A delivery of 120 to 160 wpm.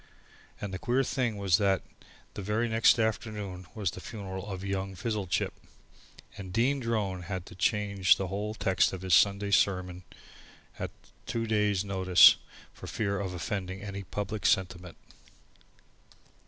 Yes: average, 140 wpm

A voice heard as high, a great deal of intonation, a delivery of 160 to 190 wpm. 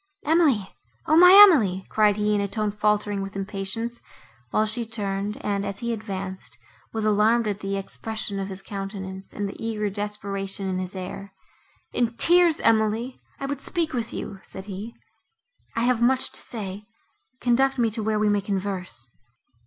No: high, 210 Hz; average, 2.9 semitones; average, 170 wpm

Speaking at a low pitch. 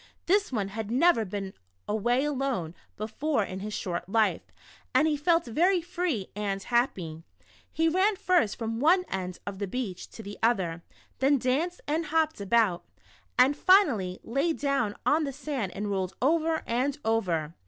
No: high, 240 Hz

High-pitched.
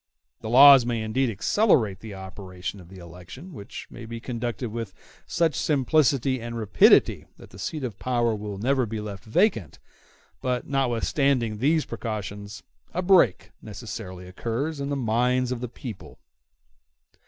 No: low, 115 Hz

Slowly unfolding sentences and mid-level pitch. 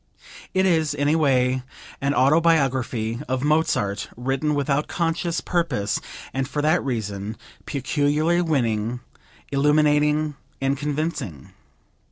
Yes: slow, 110 wpm; medium, 145 Hz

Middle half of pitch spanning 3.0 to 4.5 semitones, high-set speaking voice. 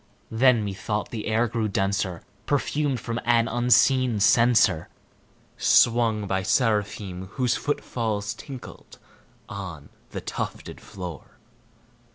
No: average, 3.3 semitones; low, 110 Hz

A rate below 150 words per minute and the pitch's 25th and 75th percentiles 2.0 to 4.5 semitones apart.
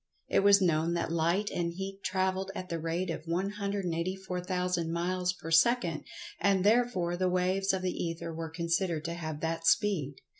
No: average, 165 wpm; narrow, 2.4 semitones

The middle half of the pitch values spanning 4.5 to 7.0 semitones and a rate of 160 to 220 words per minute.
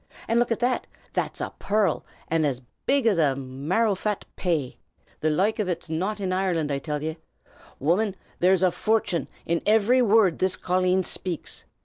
Yes: average, 5.0 semitones; average, 170 wpm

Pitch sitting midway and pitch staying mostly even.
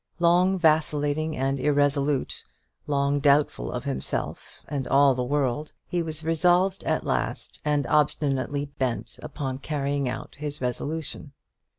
Yes: medium, 145 Hz; narrow, 2.1 semitones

